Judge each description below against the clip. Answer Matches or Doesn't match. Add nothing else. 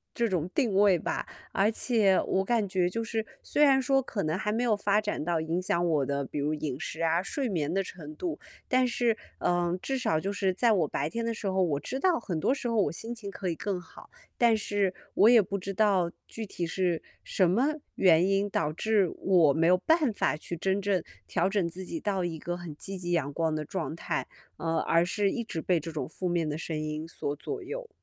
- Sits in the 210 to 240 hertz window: Doesn't match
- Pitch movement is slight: Doesn't match